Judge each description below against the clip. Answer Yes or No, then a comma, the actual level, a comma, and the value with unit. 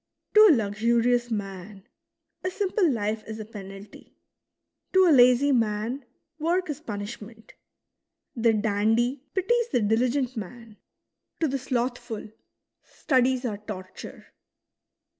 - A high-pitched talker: Yes, high, 235 Hz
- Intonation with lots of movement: No, average, 4.1 semitones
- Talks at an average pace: No, slow, 120 wpm